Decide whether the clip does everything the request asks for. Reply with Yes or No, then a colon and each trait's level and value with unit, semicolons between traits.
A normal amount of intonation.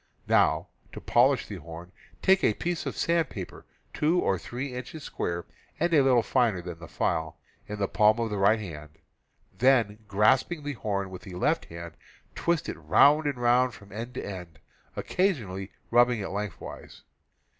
No: wide, 6.0 semitones